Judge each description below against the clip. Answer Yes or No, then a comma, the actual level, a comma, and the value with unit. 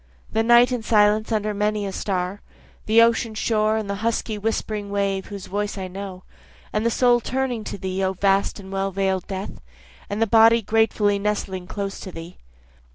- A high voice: Yes, high, 205 Hz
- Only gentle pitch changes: Yes, narrow, 2.3 semitones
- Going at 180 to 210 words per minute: Yes, average, 185 wpm